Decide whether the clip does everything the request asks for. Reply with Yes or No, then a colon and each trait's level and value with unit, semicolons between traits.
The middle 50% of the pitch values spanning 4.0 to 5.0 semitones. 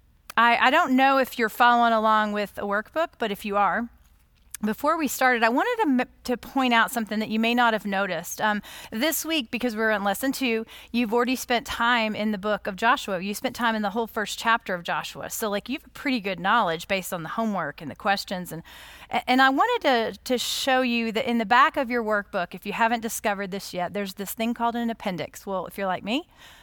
No: average, 3.5 semitones